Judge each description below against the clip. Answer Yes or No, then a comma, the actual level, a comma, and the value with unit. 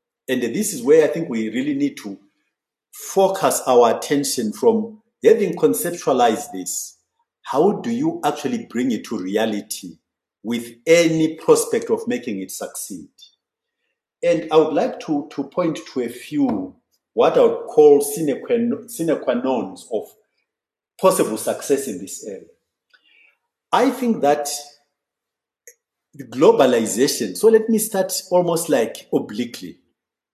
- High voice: Yes, high, 225 Hz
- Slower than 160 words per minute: Yes, average, 140 wpm